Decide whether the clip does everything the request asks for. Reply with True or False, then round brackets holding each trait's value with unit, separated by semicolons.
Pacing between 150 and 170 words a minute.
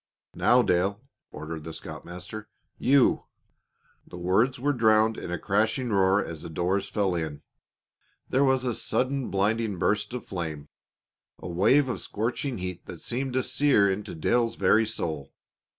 True (155 wpm)